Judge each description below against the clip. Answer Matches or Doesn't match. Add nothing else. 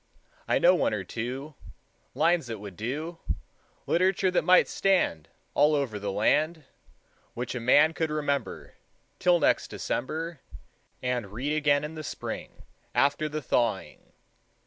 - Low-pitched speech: Doesn't match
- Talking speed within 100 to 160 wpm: Matches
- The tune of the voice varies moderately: Matches